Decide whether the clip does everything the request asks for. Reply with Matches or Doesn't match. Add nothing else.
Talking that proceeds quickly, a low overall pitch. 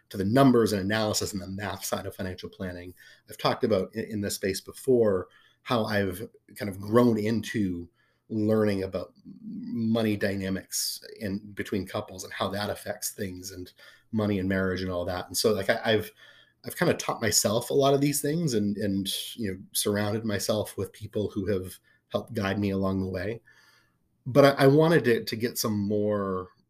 Doesn't match